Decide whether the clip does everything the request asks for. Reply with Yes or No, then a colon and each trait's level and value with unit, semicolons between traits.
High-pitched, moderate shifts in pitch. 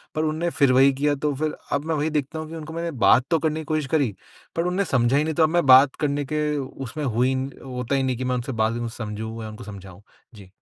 No: medium, 140 Hz; average, 4.2 semitones